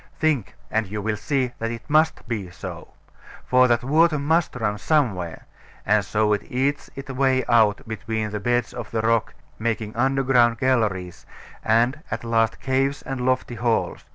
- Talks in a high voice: No, low, 120 Hz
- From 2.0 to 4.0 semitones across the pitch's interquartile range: Yes, average, 3.4 semitones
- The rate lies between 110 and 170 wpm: Yes, average, 165 wpm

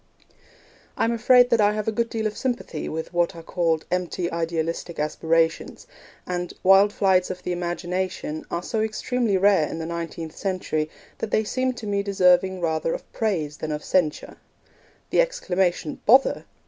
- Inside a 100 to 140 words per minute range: No, average, 170 wpm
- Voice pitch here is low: No, medium, 180 Hz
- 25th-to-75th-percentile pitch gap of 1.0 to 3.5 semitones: No, average, 4.3 semitones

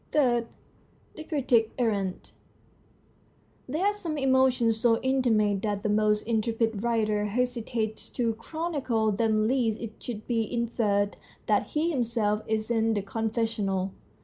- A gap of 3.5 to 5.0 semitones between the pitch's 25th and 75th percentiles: No, narrow, 2.5 semitones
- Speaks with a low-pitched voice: No, high, 225 Hz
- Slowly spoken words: Yes, slow, 130 wpm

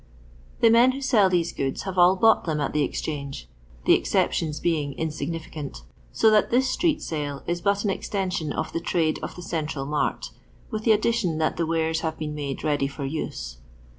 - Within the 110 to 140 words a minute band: No, average, 195 wpm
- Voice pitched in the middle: Yes, medium, 160 Hz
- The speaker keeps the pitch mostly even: No, average, 4.5 semitones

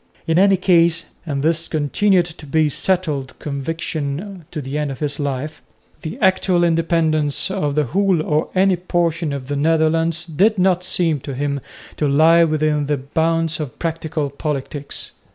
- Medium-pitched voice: Yes, medium, 160 Hz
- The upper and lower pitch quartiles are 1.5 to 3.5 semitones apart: Yes, average, 2.9 semitones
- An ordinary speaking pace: Yes, average, 165 wpm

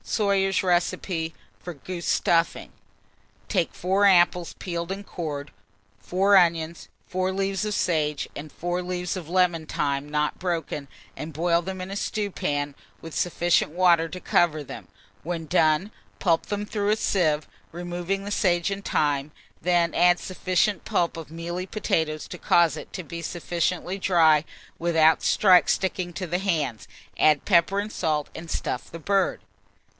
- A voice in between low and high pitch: Yes, medium, 175 Hz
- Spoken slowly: No, average, 150 wpm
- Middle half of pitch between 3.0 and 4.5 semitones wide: No, narrow, 2.6 semitones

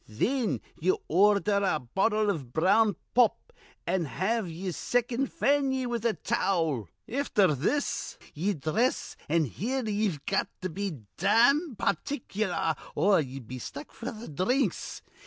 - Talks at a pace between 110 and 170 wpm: Yes, average, 140 wpm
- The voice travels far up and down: Yes, wide, 6.4 semitones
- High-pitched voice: Yes, high, 200 Hz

